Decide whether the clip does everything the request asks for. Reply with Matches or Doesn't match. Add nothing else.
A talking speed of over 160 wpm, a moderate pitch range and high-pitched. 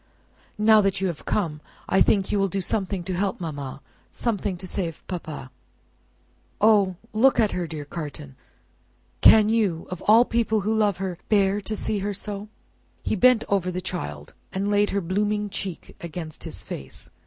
Matches